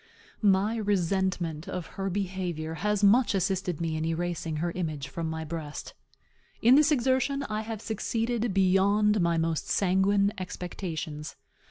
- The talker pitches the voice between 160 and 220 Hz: Yes, high, 190 Hz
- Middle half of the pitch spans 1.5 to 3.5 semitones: No, average, 4.1 semitones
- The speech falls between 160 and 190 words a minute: No, average, 140 wpm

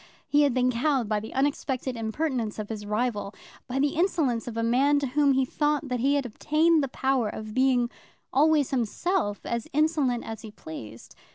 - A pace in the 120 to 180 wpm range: No, average, 190 wpm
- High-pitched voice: Yes, very high, 255 Hz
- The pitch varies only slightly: No, average, 4.2 semitones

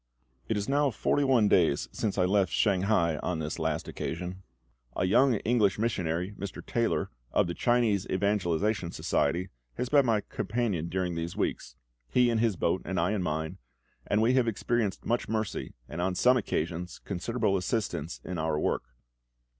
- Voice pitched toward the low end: Yes, very low, 95 Hz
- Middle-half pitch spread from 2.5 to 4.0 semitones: No, average, 4.7 semitones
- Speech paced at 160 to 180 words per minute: Yes, average, 170 wpm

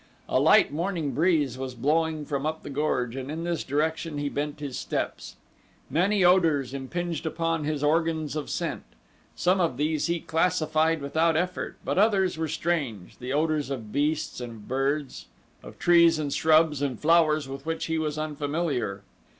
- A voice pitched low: No, medium, 155 Hz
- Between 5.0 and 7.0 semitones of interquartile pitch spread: No, average, 2.8 semitones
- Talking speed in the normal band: Yes, average, 170 wpm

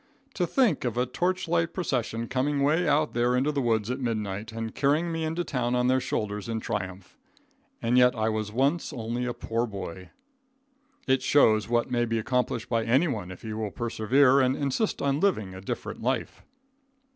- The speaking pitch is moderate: No, low, 125 Hz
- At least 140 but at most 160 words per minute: No, average, 185 wpm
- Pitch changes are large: No, average, 4.0 semitones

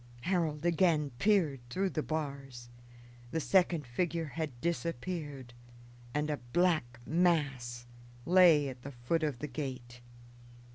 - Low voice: No, medium, 150 Hz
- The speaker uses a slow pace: Yes, slow, 125 wpm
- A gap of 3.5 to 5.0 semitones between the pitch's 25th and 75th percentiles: Yes, average, 4.7 semitones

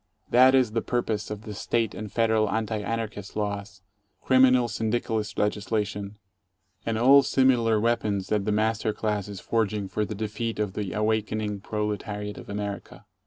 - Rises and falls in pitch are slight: Yes, narrow, 1.7 semitones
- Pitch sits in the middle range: No, low, 110 Hz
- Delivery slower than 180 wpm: Yes, average, 160 wpm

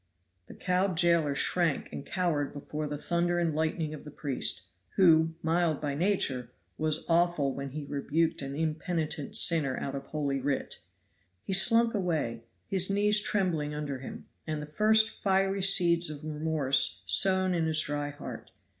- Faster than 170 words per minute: No, average, 160 wpm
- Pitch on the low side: No, medium, 160 Hz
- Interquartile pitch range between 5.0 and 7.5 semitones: No, average, 3.6 semitones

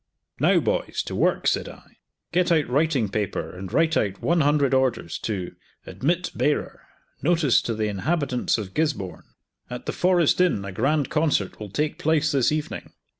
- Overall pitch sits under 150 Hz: Yes, medium, 140 Hz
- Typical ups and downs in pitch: No, wide, 6.7 semitones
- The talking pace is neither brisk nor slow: Yes, average, 170 wpm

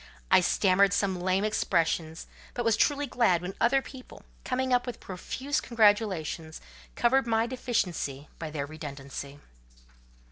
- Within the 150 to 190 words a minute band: No, slow, 135 wpm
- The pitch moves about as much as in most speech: No, wide, 6.8 semitones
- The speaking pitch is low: No, high, 200 Hz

